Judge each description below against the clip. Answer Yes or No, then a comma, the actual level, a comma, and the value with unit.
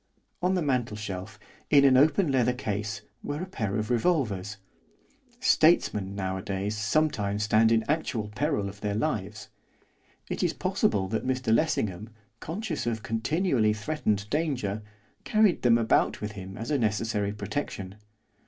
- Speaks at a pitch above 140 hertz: No, low, 110 Hz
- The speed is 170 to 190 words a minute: No, average, 140 wpm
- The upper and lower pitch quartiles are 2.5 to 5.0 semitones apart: No, wide, 5.6 semitones